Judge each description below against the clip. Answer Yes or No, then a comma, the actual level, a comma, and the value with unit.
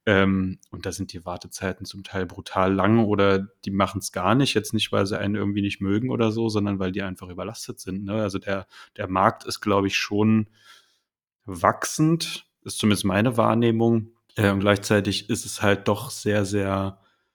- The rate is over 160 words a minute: Yes, fast, 190 wpm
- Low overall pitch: Yes, low, 100 Hz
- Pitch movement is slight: Yes, narrow, 2.0 semitones